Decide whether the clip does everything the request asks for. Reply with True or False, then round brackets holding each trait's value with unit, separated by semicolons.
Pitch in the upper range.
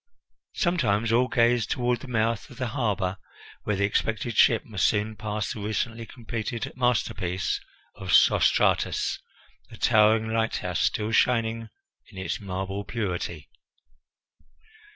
False (110 Hz)